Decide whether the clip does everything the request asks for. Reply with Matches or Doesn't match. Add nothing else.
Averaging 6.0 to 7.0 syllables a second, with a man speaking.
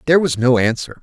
Matches